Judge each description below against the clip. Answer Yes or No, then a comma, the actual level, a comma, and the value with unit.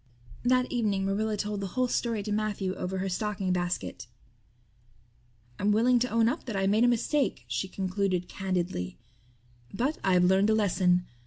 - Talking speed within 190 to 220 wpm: No, average, 165 wpm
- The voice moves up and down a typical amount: Yes, average, 3.3 semitones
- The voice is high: Yes, high, 200 Hz